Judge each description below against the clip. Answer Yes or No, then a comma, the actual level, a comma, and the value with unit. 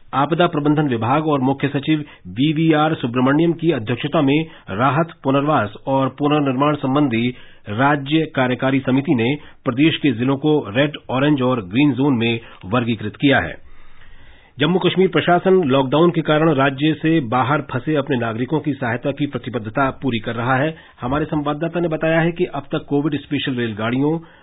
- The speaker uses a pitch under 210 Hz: Yes, medium, 140 Hz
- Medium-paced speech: Yes, average, 155 wpm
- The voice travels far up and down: No, average, 3.3 semitones